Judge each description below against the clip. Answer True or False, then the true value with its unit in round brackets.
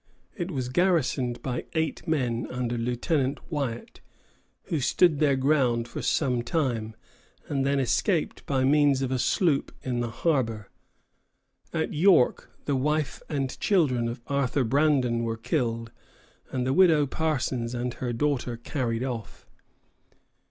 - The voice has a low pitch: True (130 Hz)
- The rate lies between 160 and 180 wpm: False (140 wpm)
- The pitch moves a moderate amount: True (3.8 semitones)